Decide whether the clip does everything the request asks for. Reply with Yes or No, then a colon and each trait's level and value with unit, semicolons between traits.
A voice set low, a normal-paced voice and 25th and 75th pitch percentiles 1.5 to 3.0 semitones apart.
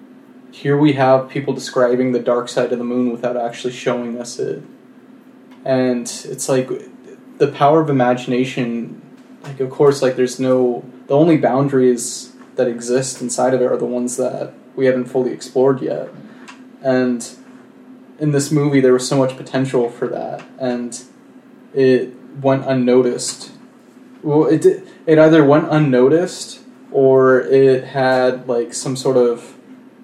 Yes: low, 130 Hz; average, 150 wpm; average, 2.7 semitones